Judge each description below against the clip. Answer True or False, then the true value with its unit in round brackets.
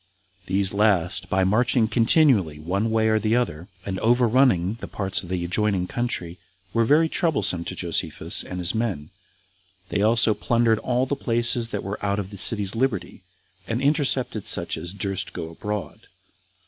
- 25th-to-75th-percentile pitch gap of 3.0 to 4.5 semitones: True (4.1 semitones)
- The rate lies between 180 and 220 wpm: False (160 wpm)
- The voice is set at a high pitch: False (105 Hz)